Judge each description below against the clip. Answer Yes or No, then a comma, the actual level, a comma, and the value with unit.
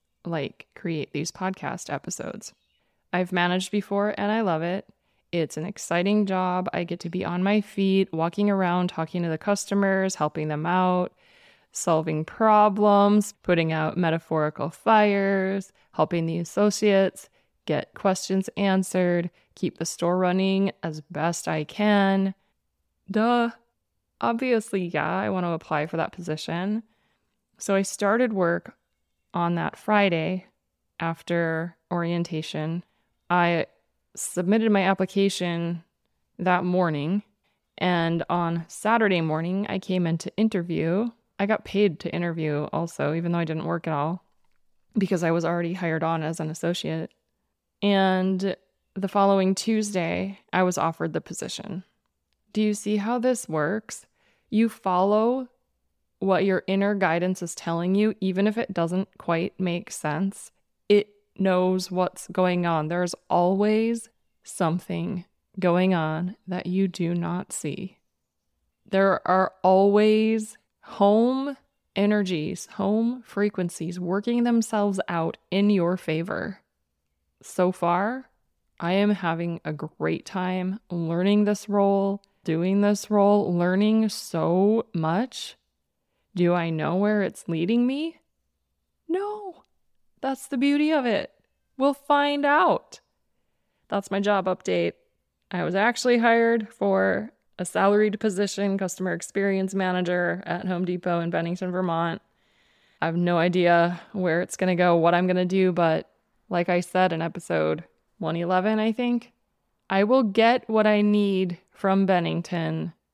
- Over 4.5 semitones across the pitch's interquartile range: No, average, 3.3 semitones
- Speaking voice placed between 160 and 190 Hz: Yes, medium, 185 Hz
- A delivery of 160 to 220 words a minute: No, slow, 135 wpm